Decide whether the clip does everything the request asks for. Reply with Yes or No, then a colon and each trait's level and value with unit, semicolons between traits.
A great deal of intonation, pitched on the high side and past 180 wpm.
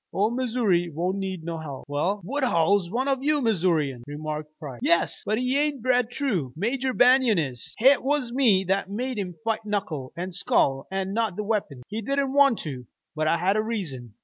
Yes: wide, 7.3 semitones; high, 200 Hz; average, 195 wpm